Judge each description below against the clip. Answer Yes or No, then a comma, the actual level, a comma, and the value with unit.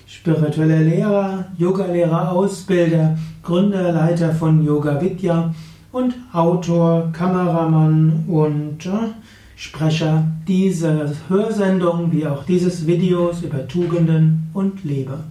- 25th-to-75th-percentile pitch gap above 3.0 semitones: No, narrow, 2.4 semitones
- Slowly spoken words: Yes, slow, 95 wpm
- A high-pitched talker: No, medium, 165 Hz